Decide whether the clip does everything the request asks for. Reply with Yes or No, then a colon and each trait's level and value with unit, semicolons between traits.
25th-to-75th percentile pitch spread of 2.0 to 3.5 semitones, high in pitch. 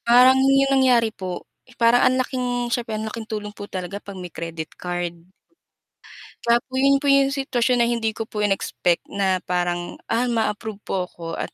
No: average, 5.1 semitones; high, 225 Hz